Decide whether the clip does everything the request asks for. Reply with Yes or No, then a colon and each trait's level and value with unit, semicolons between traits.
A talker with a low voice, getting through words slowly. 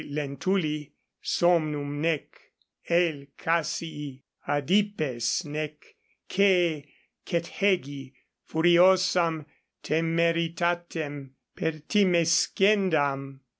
No: medium, 165 Hz; slow, 55 wpm